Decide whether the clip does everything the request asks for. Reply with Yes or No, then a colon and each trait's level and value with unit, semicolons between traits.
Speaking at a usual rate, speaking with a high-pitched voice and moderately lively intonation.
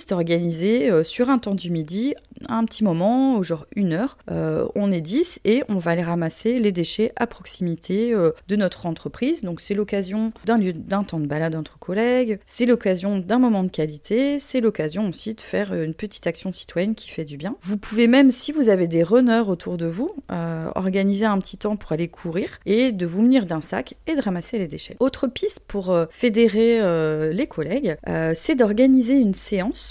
No: average, 205 wpm; high, 205 Hz; wide, 5.7 semitones